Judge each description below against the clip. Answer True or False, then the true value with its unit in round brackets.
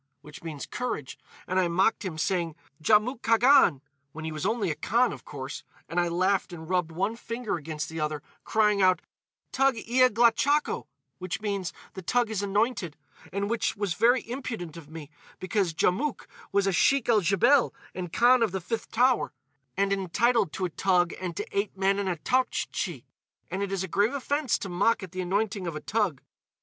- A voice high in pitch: True (195 Hz)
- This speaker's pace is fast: False (190 wpm)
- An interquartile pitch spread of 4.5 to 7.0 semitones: True (4.8 semitones)